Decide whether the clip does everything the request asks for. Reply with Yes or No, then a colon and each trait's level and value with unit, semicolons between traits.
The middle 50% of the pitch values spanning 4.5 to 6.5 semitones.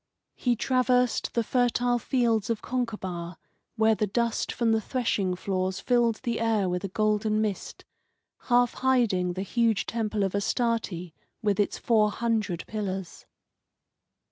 No: average, 3.3 semitones